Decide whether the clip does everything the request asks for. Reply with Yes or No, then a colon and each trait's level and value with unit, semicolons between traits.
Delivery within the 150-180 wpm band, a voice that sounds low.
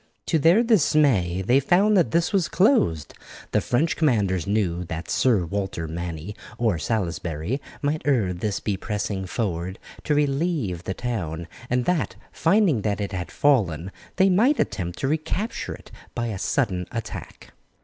Yes: average, 155 wpm; low, 110 Hz